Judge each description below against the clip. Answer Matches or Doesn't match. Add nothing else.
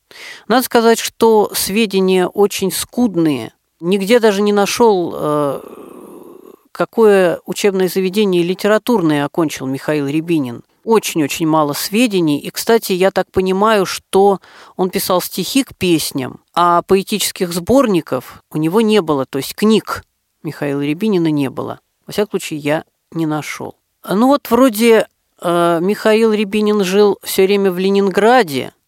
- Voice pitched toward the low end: Doesn't match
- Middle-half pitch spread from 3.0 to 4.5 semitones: Doesn't match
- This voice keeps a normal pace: Matches